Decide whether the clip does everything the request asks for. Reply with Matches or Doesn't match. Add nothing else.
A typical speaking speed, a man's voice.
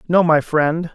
Matches